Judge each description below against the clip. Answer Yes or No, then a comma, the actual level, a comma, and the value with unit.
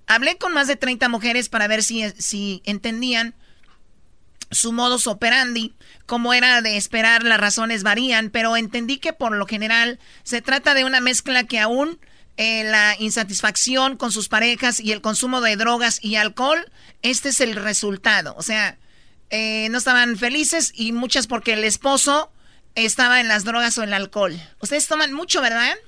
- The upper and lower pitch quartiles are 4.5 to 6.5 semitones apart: No, average, 2.8 semitones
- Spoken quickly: No, average, 170 wpm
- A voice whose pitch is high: Yes, high, 235 Hz